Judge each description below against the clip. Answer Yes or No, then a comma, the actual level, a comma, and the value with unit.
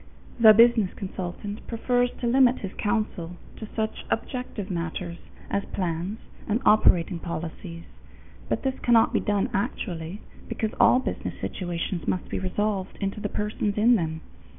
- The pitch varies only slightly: No, average, 4.0 semitones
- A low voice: No, high, 205 Hz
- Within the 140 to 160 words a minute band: Yes, average, 145 wpm